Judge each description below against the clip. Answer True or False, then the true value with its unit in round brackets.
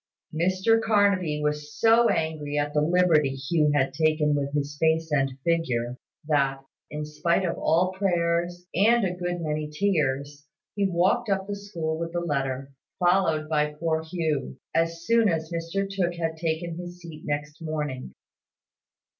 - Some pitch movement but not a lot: True (3.0 semitones)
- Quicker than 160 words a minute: False (155 wpm)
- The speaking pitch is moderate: True (160 Hz)